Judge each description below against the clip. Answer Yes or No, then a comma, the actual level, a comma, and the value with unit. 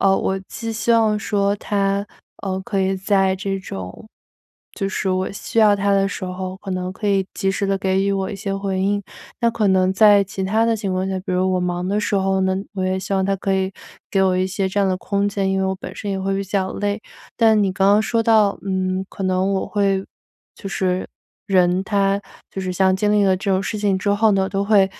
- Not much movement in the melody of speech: Yes, narrow, 1.3 semitones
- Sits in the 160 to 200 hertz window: Yes, high, 195 Hz